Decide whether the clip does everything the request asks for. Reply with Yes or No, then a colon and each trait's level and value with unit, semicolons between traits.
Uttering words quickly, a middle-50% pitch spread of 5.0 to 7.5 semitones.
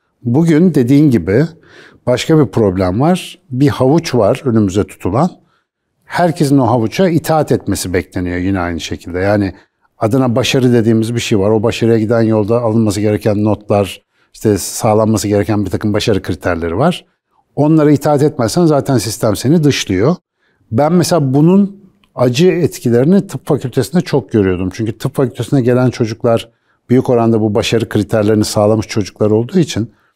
Yes: fast, 145 wpm; average, 5.3 semitones